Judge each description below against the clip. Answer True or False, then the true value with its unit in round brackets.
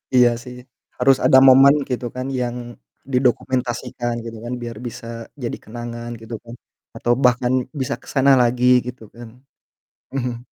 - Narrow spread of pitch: True (1.3 semitones)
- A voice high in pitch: False (125 Hz)